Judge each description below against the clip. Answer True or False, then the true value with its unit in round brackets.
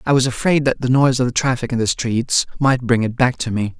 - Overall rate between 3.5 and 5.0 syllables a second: False (5.9 syllables/s)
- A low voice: True (125 Hz)